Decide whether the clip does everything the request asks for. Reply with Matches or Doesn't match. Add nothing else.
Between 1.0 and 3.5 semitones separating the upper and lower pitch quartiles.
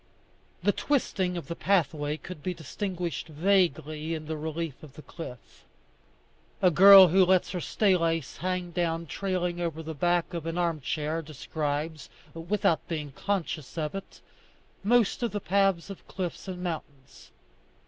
Matches